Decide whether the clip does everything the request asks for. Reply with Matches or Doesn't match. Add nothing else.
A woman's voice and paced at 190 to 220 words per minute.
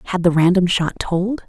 Matches